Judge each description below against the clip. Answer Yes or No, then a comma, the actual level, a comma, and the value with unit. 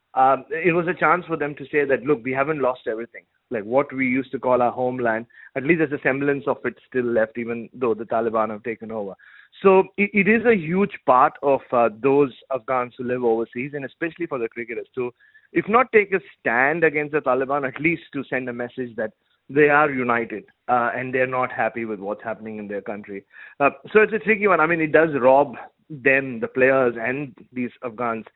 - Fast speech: Yes, fast, 220 wpm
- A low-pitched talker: Yes, low, 130 Hz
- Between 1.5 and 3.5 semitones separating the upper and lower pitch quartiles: No, average, 4.7 semitones